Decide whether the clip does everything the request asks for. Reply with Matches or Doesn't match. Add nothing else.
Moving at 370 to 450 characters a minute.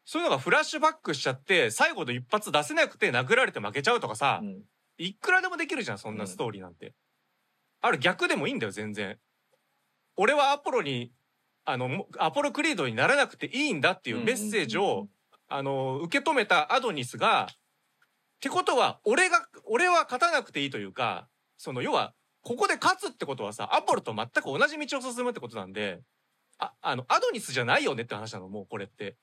Matches